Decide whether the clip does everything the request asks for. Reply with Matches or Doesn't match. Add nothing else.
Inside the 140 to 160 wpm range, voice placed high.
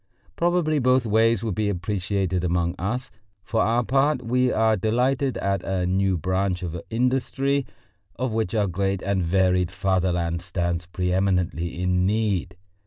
Doesn't match